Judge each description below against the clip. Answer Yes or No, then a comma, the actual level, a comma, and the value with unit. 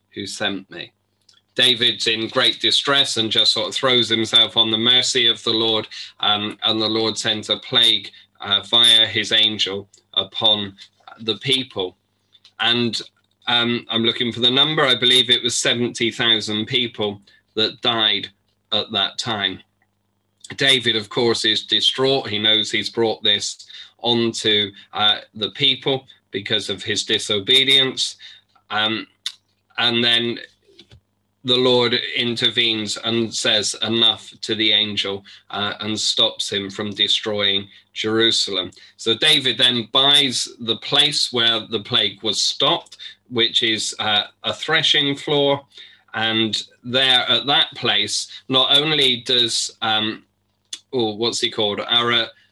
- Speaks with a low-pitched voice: Yes, low, 115 Hz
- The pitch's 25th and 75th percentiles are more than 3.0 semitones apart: No, narrow, 2.6 semitones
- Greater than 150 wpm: No, slow, 135 wpm